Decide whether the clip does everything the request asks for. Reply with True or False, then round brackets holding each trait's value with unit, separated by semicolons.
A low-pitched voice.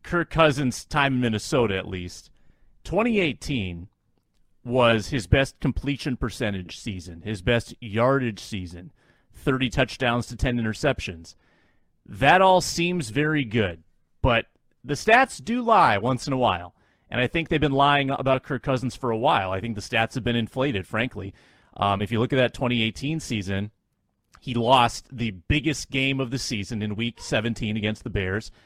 True (120 Hz)